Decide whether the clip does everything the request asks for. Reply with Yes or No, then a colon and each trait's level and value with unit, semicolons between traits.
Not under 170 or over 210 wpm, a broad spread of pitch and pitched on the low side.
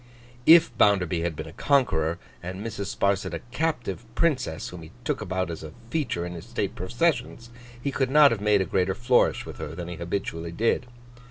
Yes: average, 195 wpm; wide, 6.1 semitones; low, 100 Hz